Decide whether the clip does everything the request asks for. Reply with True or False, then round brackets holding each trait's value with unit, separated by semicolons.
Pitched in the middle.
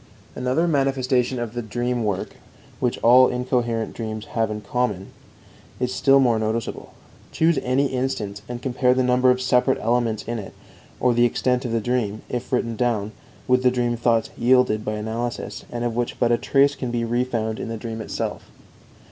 False (120 Hz)